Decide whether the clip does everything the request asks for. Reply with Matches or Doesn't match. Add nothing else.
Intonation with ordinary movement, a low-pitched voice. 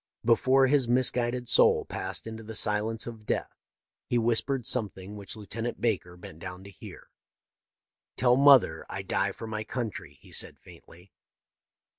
Matches